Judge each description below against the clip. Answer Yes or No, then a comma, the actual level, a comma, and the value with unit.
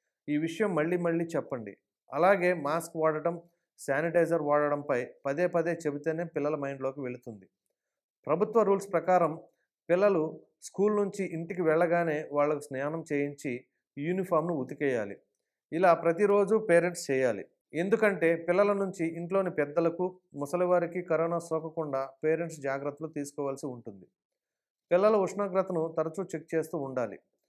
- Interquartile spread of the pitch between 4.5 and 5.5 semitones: No, average, 3.4 semitones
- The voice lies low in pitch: No, medium, 165 Hz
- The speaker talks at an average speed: No, slow, 110 wpm